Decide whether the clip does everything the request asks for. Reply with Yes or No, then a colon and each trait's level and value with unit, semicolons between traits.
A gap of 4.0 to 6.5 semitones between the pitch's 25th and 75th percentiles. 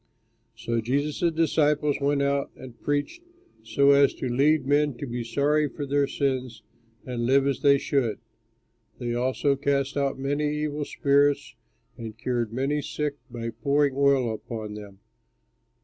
No: average, 3.1 semitones